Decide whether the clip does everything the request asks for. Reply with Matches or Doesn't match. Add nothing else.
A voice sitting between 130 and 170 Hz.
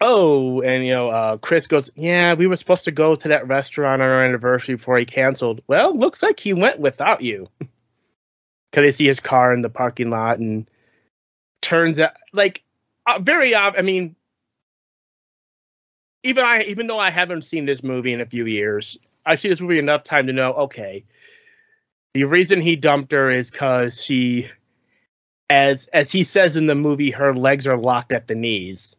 Matches